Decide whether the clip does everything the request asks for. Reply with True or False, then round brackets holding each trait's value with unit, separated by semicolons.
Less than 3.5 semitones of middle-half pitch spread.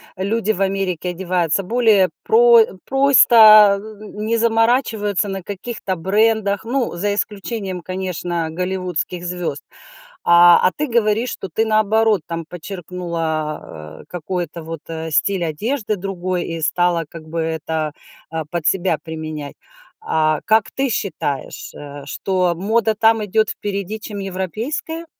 False (4.5 semitones)